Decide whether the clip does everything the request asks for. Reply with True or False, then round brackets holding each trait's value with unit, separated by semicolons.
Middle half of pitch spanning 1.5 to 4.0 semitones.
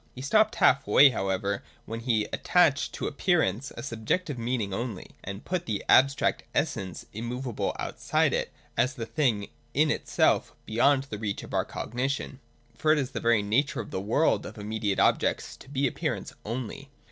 False (4.5 semitones)